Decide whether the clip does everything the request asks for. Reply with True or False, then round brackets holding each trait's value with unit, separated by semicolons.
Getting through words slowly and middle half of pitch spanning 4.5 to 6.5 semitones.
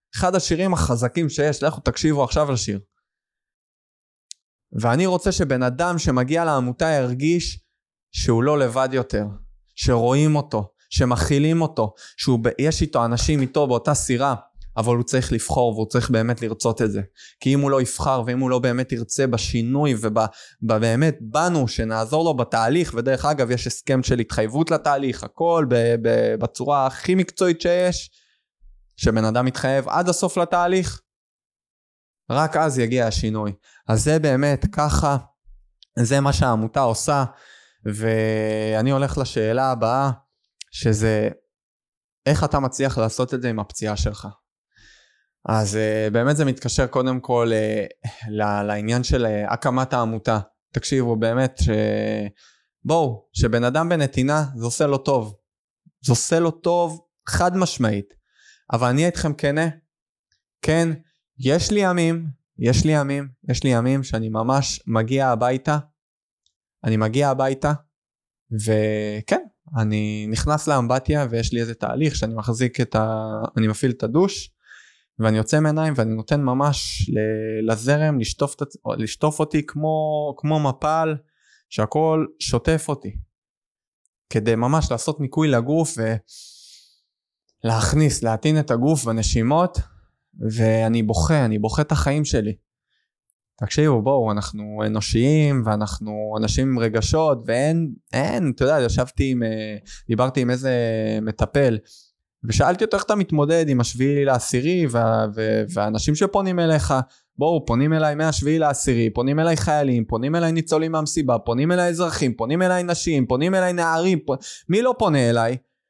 False (130 wpm; 5.3 semitones)